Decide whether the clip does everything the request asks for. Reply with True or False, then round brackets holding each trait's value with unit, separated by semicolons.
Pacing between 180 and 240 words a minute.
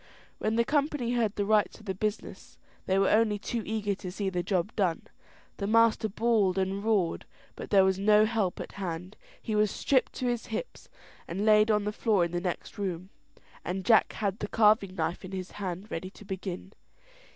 True (200 wpm)